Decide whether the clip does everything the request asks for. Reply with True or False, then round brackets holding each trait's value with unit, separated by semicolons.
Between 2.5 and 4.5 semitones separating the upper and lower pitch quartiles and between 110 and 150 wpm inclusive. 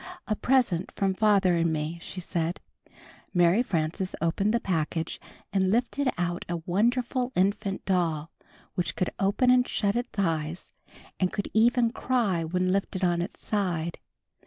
True (3.8 semitones; 145 wpm)